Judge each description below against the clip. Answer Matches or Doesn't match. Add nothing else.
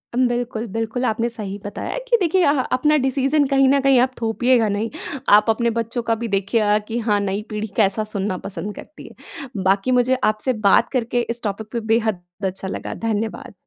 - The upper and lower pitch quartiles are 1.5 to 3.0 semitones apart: Doesn't match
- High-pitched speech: Matches